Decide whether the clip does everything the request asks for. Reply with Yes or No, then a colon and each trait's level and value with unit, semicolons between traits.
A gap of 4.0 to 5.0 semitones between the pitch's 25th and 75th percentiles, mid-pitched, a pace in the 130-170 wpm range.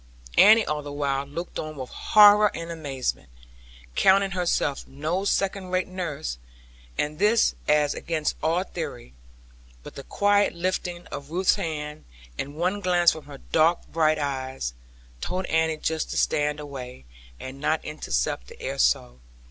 Yes: average, 4.3 semitones; medium, 155 Hz; average, 150 wpm